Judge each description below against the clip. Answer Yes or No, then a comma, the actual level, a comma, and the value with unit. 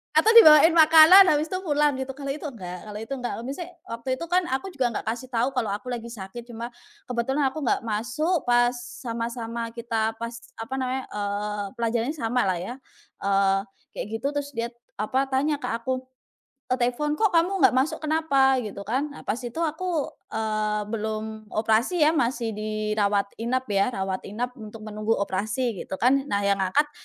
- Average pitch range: Yes, average, 4.5 semitones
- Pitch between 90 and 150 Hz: No, high, 240 Hz